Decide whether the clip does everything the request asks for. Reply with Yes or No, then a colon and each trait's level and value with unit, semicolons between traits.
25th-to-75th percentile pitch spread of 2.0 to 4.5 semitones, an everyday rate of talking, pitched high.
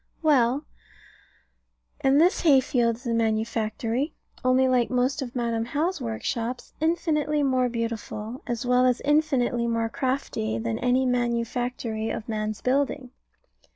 No: average, 2.8 semitones; slow, 130 wpm; high, 245 Hz